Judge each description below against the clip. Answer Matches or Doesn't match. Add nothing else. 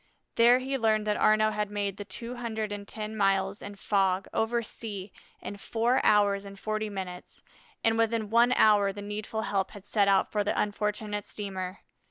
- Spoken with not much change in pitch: Matches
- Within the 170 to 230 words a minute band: Matches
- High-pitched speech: Matches